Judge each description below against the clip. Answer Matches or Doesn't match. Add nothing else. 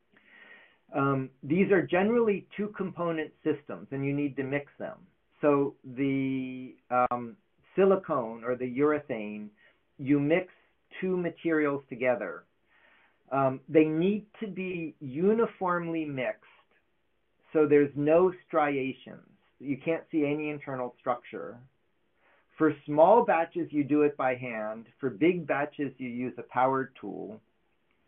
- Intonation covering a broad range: Doesn't match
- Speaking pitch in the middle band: Matches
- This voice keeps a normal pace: Doesn't match